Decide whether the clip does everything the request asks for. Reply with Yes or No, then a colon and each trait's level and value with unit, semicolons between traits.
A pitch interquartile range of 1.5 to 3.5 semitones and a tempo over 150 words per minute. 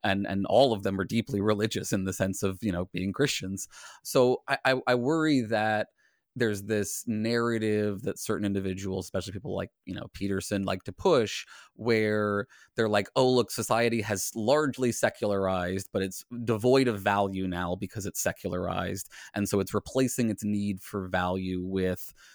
Yes: average, 3.0 semitones; average, 170 wpm